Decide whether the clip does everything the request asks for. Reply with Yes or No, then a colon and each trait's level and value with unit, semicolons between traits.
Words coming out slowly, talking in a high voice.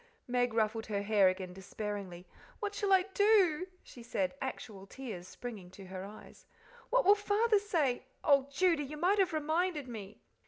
No: average, 165 wpm; very high, 260 Hz